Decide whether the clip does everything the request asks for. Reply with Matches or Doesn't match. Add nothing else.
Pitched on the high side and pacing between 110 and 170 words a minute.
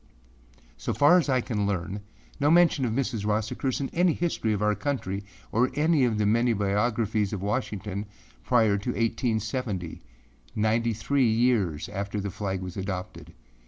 Doesn't match